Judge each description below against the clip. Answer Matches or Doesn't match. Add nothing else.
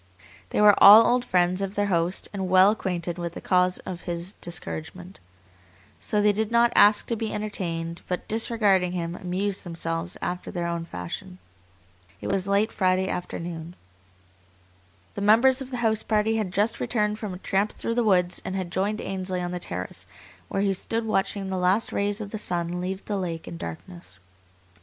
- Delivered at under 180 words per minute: Doesn't match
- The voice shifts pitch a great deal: Doesn't match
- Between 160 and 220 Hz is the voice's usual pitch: Matches